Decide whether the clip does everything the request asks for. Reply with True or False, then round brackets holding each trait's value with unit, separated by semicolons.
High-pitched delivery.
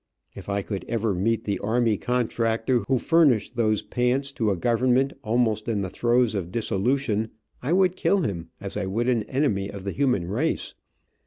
False (115 Hz)